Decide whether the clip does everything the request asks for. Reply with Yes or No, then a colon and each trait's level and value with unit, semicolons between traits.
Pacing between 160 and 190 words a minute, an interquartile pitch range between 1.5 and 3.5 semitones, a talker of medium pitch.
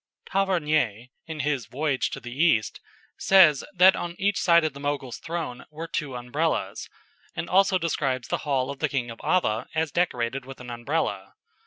No: average, 175 wpm; average, 5.1 semitones; medium, 145 Hz